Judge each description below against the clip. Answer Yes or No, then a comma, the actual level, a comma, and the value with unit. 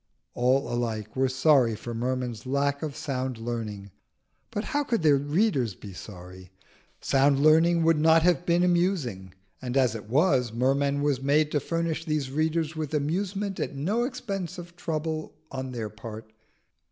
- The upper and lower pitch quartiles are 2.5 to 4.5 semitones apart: No, average, 5.3 semitones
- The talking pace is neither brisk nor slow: Yes, average, 160 wpm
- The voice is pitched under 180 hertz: Yes, medium, 140 Hz